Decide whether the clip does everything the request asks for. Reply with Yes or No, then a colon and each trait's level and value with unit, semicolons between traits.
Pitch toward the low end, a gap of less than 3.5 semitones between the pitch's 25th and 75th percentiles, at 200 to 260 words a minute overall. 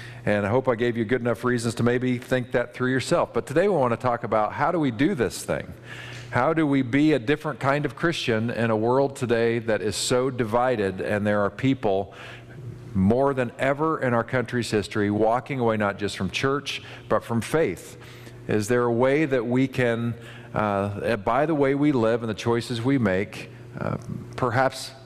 Yes: low, 120 Hz; narrow, 2.5 semitones; fast, 205 wpm